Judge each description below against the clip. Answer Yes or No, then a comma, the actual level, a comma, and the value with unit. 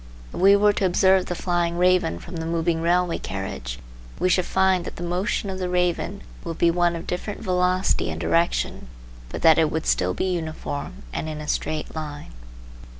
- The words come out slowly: No, average, 195 wpm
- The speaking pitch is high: No, medium, 175 Hz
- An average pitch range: No, narrow, 2.3 semitones